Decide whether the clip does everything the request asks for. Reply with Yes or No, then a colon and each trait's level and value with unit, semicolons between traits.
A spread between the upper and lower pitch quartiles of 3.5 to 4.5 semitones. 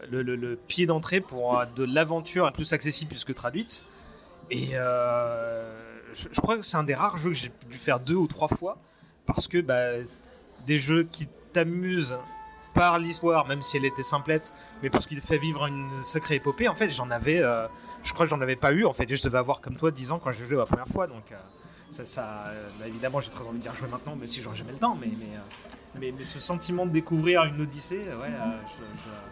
No: average, 5.0 semitones